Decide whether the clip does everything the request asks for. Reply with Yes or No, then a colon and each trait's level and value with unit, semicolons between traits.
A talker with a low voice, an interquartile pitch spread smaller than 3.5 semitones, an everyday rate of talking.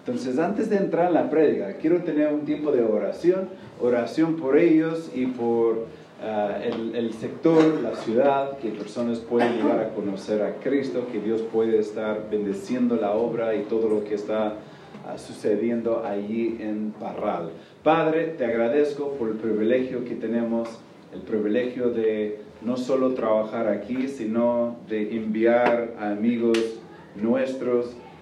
Yes: low, 115 Hz; average, 2.8 semitones; average, 150 wpm